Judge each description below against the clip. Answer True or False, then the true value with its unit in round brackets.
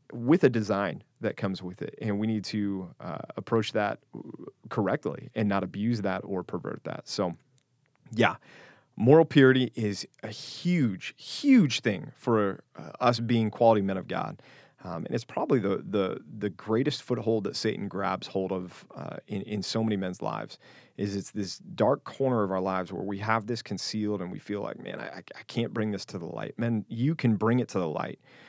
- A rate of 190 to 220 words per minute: True (200 wpm)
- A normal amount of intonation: True (3.3 semitones)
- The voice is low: True (110 Hz)